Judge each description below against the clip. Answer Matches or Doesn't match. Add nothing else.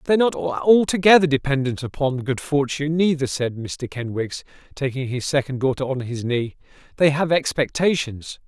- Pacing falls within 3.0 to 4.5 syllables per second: Doesn't match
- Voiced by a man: Matches